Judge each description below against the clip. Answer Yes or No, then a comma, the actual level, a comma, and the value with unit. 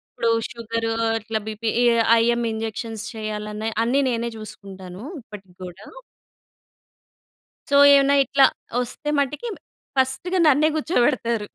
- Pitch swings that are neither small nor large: Yes, average, 3.6 semitones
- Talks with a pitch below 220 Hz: No, high, 230 Hz